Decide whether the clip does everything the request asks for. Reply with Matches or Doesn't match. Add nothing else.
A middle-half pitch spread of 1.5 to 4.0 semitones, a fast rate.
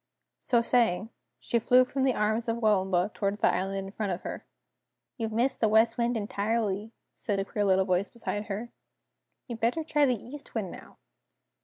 Doesn't match